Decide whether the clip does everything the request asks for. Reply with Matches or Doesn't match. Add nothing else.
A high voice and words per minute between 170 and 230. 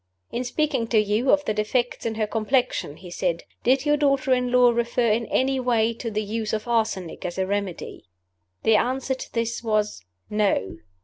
Matches